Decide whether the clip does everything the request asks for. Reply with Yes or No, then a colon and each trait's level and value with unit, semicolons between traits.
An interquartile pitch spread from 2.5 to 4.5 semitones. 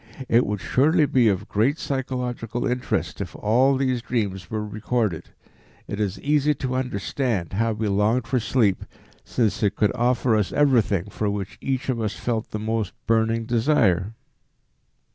Yes: average, 3.5 semitones